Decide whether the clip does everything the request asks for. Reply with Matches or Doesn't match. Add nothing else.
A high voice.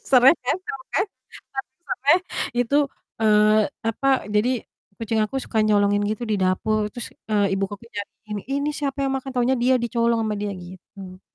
Matches